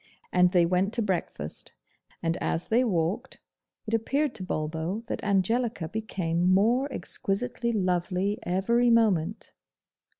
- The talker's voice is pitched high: Yes, high, 195 Hz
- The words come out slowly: Yes, slow, 125 wpm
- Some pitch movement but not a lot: Yes, average, 4.6 semitones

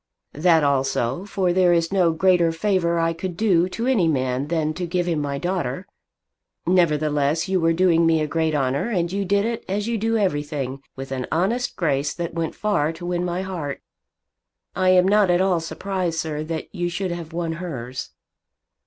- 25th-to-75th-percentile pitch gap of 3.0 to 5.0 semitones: Yes, average, 3.4 semitones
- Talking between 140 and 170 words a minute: No, average, 190 wpm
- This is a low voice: No, medium, 170 Hz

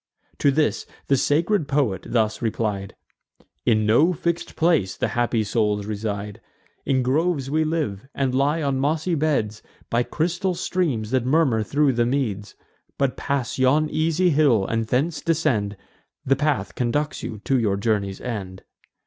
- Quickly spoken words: No, average, 150 wpm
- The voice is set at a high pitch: No, low, 130 Hz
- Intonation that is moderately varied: No, wide, 6.1 semitones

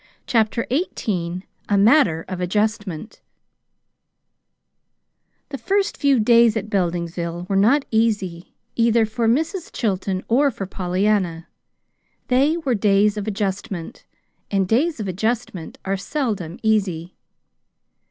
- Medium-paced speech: No, slow, 115 wpm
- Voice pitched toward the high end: Yes, high, 210 Hz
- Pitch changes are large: No, average, 4.1 semitones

